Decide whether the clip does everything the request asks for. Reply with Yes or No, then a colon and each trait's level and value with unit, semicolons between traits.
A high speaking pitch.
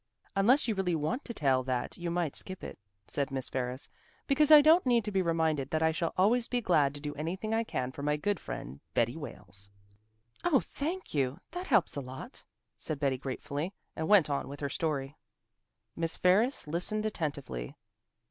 No: medium, 160 Hz